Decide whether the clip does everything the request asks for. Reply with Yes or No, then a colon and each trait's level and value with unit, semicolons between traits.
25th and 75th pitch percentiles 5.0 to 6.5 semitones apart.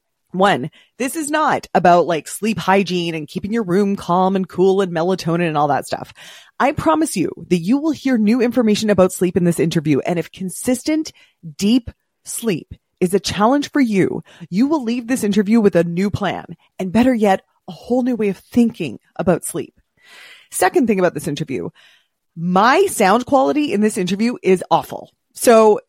Yes: wide, 5.5 semitones